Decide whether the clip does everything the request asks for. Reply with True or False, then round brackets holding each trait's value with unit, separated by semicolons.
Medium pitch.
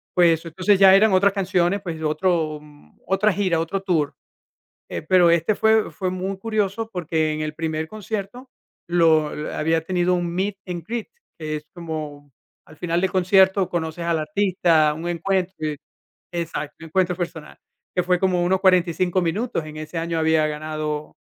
True (175 Hz)